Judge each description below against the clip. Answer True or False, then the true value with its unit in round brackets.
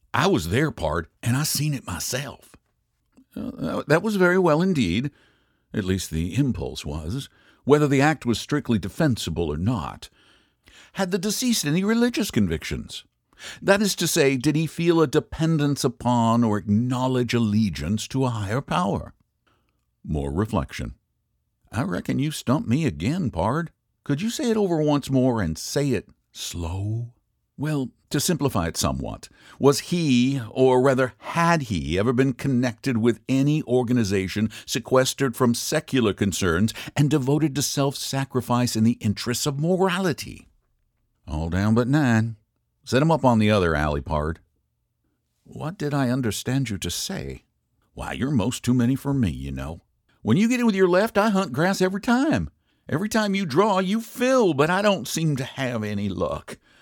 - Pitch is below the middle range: True (130 Hz)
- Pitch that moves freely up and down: True (6.4 semitones)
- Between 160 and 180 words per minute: True (165 wpm)